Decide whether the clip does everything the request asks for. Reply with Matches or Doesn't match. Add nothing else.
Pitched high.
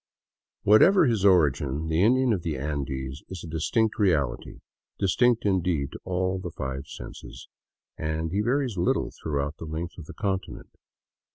Doesn't match